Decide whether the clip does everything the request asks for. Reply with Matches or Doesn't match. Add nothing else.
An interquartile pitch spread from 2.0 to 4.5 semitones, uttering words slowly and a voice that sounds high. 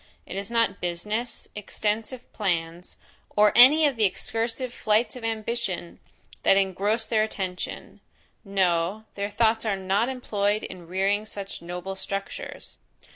Matches